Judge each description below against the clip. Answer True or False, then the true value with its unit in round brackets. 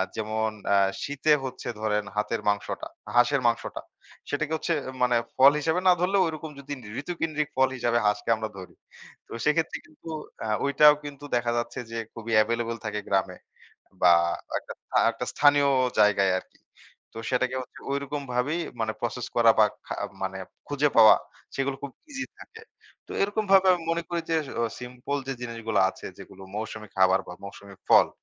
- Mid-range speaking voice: False (125 Hz)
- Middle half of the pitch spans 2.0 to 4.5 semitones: False (5.1 semitones)